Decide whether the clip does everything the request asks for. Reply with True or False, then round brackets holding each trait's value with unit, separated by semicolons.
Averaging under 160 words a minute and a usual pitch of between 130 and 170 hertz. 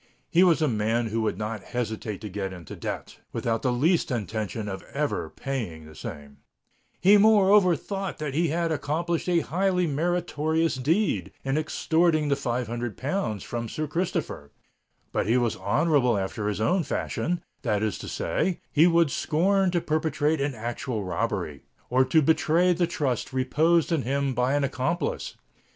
False (165 wpm; 140 Hz)